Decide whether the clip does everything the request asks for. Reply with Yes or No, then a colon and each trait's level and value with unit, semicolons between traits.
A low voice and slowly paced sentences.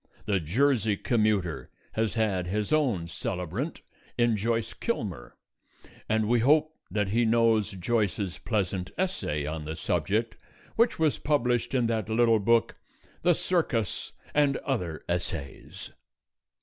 Yes: low, 110 Hz; slow, 125 wpm